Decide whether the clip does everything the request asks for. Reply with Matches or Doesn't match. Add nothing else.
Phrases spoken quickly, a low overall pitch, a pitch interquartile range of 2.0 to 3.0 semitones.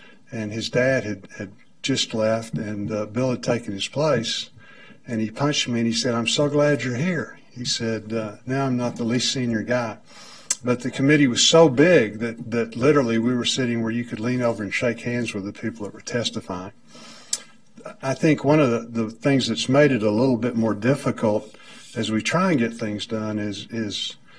Matches